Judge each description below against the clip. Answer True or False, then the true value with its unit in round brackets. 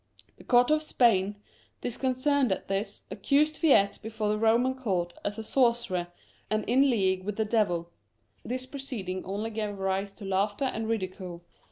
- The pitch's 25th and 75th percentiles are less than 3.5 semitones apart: False (4.6 semitones)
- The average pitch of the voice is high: True (215 Hz)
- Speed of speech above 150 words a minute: True (160 wpm)